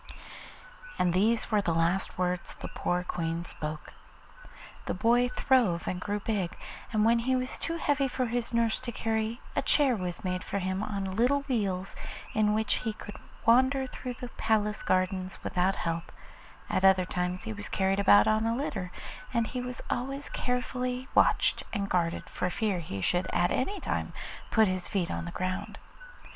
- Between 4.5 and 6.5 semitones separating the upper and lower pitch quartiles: Yes, average, 5.0 semitones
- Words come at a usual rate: Yes, average, 180 wpm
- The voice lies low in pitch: No, high, 210 Hz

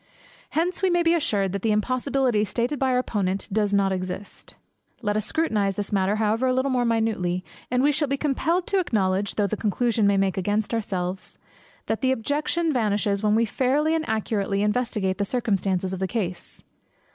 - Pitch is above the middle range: Yes, high, 215 Hz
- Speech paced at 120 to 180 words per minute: No, average, 190 wpm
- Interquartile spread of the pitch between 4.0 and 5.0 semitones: Yes, average, 4.7 semitones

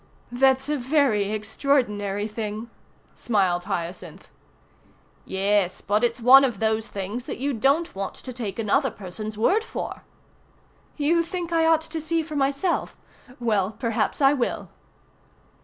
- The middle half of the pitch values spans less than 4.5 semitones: No, wide, 5.4 semitones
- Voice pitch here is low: No, high, 235 Hz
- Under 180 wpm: Yes, average, 140 wpm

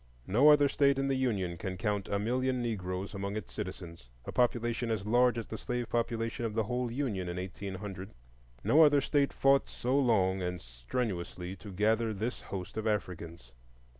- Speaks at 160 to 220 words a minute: Yes, average, 175 wpm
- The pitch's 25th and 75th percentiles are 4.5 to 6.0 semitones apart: Yes, average, 4.8 semitones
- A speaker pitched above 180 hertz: No, low, 110 Hz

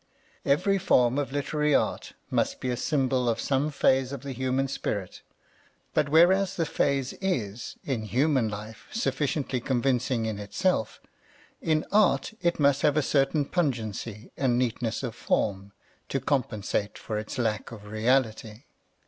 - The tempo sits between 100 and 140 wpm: No, average, 150 wpm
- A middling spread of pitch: Yes, average, 4.5 semitones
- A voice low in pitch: Yes, low, 130 Hz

